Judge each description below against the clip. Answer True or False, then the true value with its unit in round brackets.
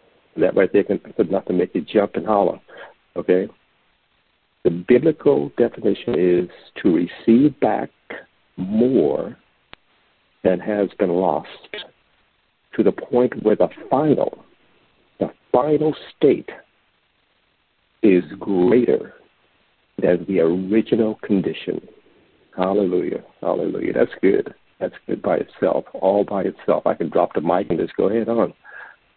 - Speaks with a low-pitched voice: True (125 Hz)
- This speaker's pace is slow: True (125 wpm)